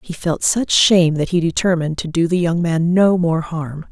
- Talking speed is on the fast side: Yes, fast, 230 wpm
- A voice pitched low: No, medium, 170 Hz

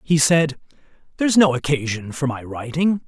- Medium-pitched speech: Yes, medium, 145 Hz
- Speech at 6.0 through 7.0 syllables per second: No, 5.1 syllables/s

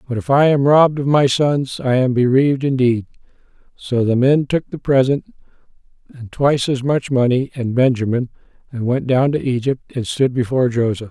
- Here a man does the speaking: Yes, male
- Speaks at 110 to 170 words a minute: No, average, 185 wpm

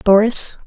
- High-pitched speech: Yes, high, 215 Hz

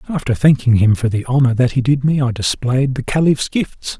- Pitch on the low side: Yes, low, 130 Hz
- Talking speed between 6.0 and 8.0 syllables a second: No, 5.3 syllables/s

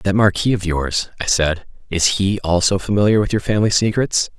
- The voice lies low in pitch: Yes, very low, 95 Hz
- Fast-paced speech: No, average, 190 wpm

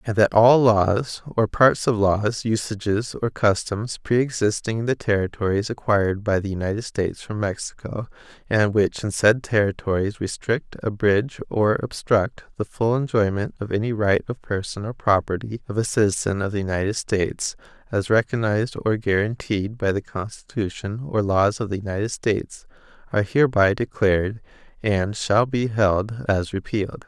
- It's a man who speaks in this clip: Yes, male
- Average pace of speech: Yes, average, 155 wpm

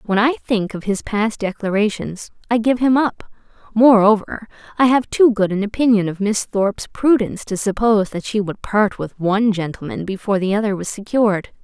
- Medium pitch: No, high, 210 Hz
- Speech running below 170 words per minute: No, average, 185 wpm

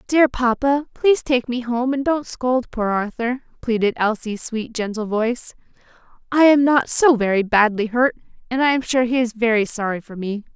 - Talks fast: No, average, 190 wpm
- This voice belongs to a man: No, female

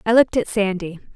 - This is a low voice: No, high, 205 Hz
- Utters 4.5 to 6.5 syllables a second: No, 6.7 syllables/s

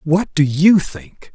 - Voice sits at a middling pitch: Yes, medium, 160 Hz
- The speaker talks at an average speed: Yes, average, 180 wpm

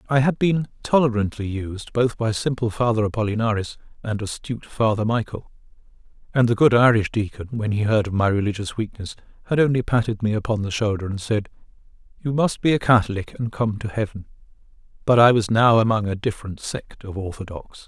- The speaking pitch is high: No, low, 110 Hz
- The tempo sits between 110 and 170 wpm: No, average, 180 wpm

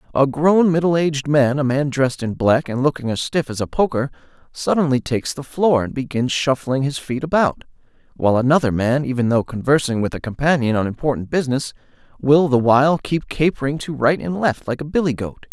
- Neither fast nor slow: Yes, average, 195 wpm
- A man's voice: Yes, male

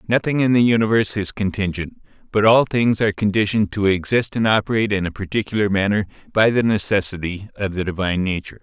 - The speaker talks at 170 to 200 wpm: Yes, average, 180 wpm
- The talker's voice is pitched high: No, low, 100 Hz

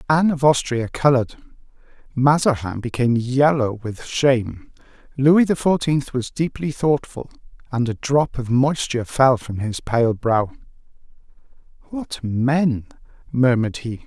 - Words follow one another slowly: Yes, slow, 125 wpm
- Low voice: Yes, low, 130 Hz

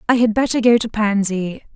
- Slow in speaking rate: No, fast, 205 wpm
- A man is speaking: No, female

